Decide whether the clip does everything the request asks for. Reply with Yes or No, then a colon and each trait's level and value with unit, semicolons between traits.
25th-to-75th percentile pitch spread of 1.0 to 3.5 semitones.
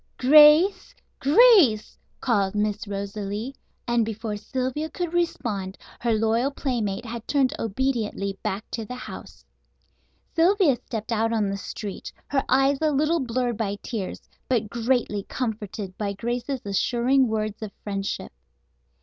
No: average, 4.3 semitones